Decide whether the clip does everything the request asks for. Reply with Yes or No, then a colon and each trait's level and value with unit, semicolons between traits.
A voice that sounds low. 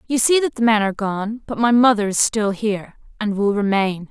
No: high, 215 Hz